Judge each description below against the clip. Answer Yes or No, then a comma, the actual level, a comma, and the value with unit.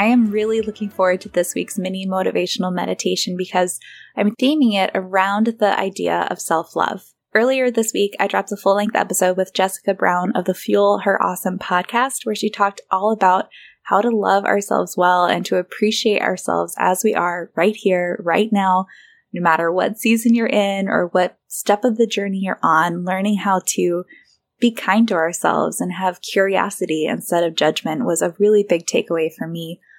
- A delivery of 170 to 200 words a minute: Yes, average, 190 wpm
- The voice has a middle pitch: No, high, 195 Hz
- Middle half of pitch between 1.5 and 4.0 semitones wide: Yes, average, 2.7 semitones